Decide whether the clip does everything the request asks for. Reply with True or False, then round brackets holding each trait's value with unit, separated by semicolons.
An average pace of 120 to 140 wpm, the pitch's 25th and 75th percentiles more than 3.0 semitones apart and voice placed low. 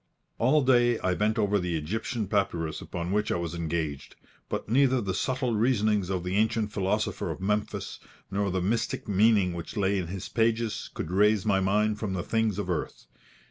False (185 wpm; 3.4 semitones; 105 Hz)